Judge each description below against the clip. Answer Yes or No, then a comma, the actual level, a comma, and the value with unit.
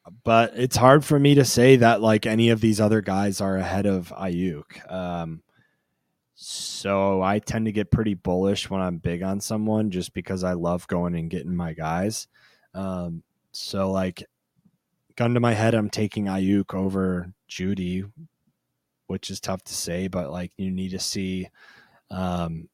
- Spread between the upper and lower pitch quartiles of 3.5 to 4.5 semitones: No, average, 3.0 semitones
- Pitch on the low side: Yes, very low, 95 Hz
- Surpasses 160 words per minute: Yes, average, 170 wpm